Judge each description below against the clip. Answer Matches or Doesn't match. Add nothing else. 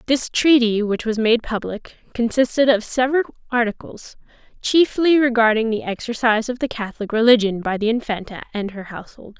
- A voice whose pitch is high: Matches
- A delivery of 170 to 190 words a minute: Doesn't match